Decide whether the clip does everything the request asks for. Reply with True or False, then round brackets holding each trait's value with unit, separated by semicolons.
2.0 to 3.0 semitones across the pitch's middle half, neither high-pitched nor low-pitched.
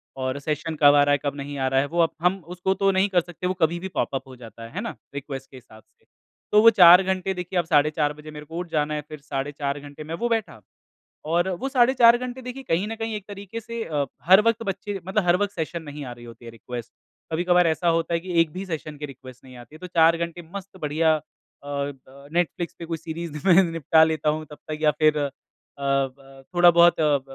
False (4.1 semitones; 160 Hz)